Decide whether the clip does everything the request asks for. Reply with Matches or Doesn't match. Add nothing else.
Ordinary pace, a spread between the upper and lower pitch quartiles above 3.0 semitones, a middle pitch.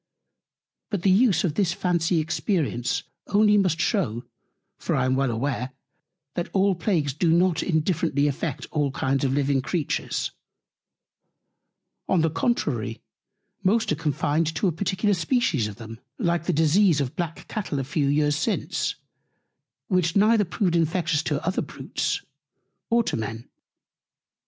Matches